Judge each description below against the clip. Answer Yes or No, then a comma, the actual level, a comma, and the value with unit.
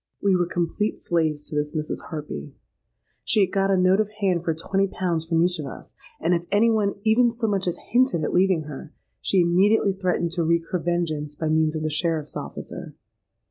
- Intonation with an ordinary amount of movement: Yes, average, 3.6 semitones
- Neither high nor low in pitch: Yes, medium, 175 Hz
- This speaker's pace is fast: Yes, fast, 210 wpm